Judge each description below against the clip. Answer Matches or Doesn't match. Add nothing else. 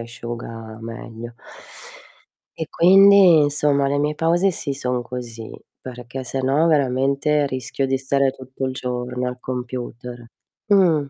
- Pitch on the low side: Matches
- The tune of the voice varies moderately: Matches